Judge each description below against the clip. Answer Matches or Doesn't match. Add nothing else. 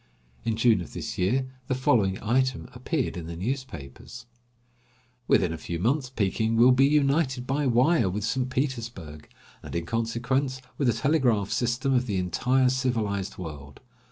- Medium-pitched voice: Doesn't match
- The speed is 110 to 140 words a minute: Doesn't match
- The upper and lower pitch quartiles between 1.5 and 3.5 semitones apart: Doesn't match